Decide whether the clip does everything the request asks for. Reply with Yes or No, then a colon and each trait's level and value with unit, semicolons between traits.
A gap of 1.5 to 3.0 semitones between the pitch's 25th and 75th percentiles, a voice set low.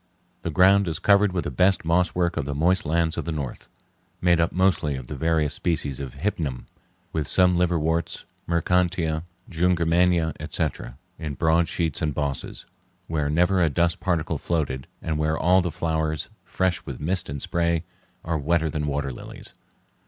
Yes: narrow, 2.6 semitones; very low, 80 Hz